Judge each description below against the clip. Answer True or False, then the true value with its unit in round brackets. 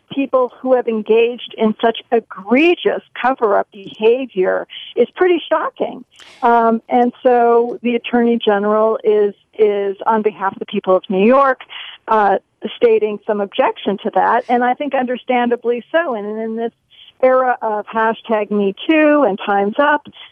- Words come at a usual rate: True (150 wpm)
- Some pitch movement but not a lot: True (3.0 semitones)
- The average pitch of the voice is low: False (230 Hz)